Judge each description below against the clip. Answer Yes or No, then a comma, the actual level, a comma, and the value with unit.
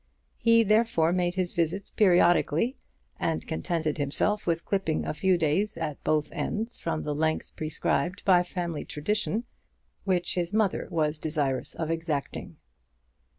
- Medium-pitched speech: Yes, medium, 170 Hz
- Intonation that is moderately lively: Yes, average, 3.7 semitones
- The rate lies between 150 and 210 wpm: No, average, 140 wpm